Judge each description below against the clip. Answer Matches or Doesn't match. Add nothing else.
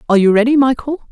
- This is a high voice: Matches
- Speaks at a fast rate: Matches